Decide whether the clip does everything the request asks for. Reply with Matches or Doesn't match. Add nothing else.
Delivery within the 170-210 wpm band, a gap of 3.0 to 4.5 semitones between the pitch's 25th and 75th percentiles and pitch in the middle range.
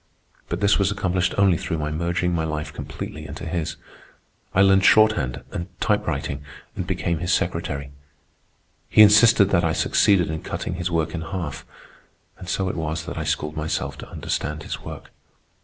Doesn't match